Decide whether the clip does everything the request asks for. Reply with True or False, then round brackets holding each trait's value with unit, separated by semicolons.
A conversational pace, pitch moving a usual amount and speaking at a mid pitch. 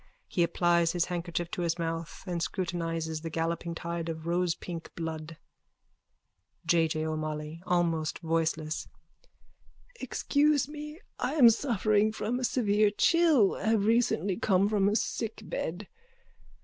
False (125 wpm; 4.5 semitones; 175 Hz)